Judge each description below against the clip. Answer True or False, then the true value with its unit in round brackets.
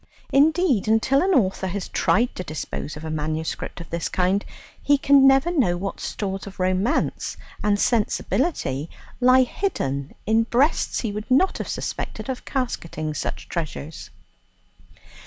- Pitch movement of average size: False (7.8 semitones)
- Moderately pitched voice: False (210 Hz)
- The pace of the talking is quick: False (145 wpm)